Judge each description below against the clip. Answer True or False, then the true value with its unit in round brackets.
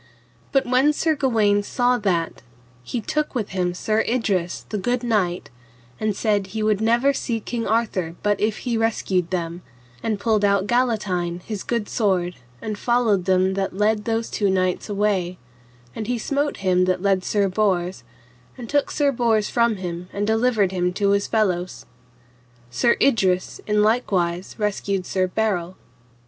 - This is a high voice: True (205 Hz)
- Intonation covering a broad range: False (3.8 semitones)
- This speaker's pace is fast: False (165 wpm)